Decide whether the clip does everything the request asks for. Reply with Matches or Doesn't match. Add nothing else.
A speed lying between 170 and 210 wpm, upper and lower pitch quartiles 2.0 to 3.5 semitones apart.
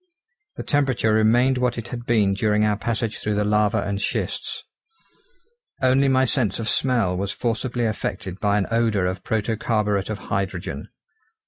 Doesn't match